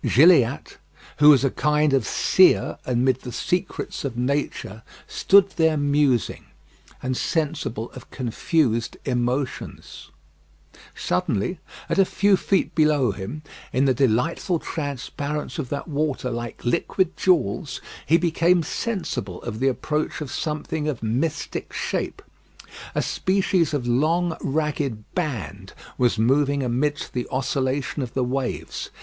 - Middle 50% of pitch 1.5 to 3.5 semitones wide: No, average, 4.2 semitones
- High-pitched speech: No, medium, 140 Hz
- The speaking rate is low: Yes, slow, 130 wpm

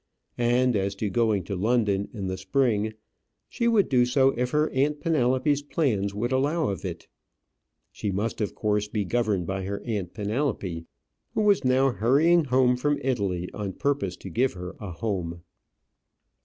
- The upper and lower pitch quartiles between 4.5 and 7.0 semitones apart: Yes, average, 5.3 semitones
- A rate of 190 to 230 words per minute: No, average, 170 wpm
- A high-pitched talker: No, low, 115 Hz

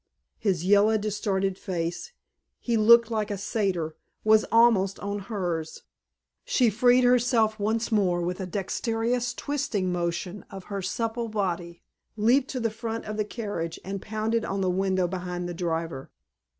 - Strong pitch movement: No, average, 3.8 semitones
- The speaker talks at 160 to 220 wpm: No, average, 150 wpm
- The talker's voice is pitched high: Yes, high, 205 Hz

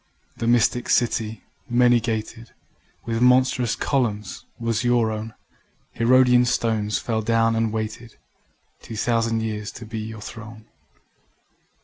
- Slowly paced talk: Yes, slow, 120 wpm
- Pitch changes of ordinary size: No, narrow, 1.6 semitones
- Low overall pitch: Yes, low, 115 Hz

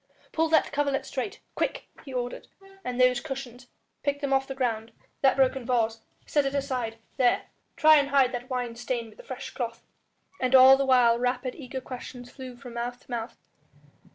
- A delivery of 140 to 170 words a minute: No, average, 185 wpm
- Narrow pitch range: Yes, narrow, 1.9 semitones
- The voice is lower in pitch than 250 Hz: No, very high, 255 Hz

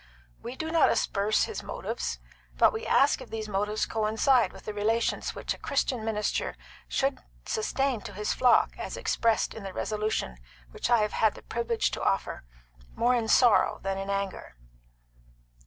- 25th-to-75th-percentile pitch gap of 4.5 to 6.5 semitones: No, average, 3.1 semitones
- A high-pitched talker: Yes, high, 220 Hz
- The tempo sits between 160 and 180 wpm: Yes, average, 170 wpm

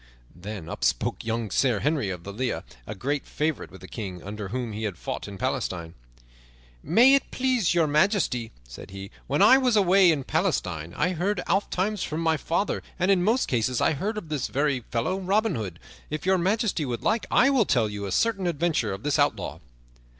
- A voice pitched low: No, medium, 150 Hz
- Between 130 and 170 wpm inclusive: No, average, 200 wpm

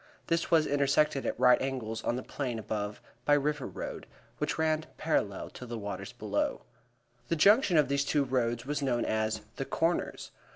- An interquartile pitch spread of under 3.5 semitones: No, average, 4.3 semitones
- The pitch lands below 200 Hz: Yes, low, 135 Hz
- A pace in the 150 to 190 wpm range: Yes, average, 175 wpm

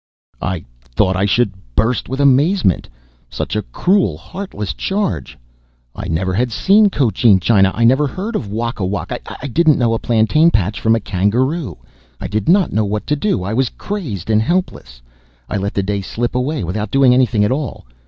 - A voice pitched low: Yes, low, 115 Hz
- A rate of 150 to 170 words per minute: No, average, 185 wpm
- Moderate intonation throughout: No, wide, 6.3 semitones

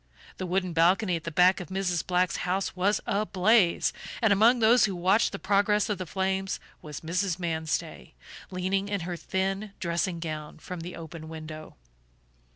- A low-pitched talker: No, medium, 185 Hz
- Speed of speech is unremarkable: Yes, average, 165 wpm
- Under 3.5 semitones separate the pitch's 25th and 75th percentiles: Yes, average, 2.7 semitones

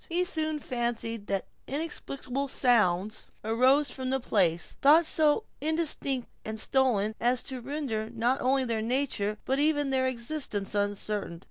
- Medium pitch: No, very high, 255 Hz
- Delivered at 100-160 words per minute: Yes, average, 140 wpm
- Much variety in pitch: No, average, 4.5 semitones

